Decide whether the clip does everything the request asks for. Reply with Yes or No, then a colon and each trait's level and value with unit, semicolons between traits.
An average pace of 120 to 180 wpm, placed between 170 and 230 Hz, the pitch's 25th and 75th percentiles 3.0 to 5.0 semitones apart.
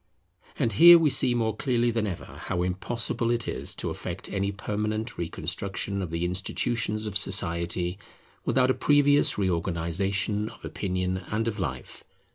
No: average, 150 wpm; low, 100 Hz; average, 4.2 semitones